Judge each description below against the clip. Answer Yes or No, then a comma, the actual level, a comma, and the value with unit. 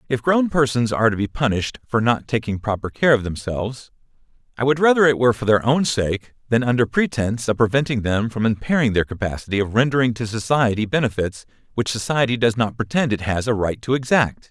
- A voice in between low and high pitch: No, low, 120 Hz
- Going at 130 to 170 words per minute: No, fast, 205 wpm